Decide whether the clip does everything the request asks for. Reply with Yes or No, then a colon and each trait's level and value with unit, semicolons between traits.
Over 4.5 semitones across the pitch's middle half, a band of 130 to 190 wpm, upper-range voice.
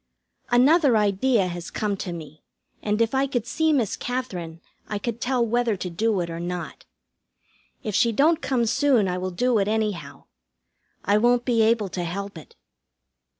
Yes: average, 5.0 semitones; average, 175 wpm; high, 215 Hz